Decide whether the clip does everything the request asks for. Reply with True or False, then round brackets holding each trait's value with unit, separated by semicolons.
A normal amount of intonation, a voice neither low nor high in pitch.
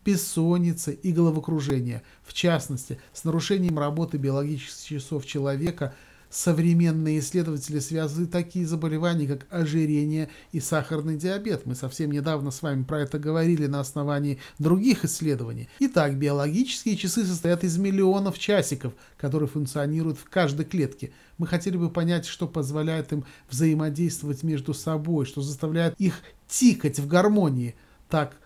True (3.0 semitones; 155 Hz)